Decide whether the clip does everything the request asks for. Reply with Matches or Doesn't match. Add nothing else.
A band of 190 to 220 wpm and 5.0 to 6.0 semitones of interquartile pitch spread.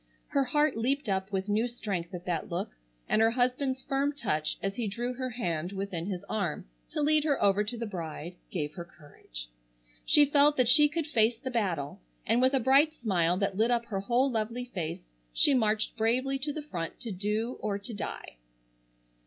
Matches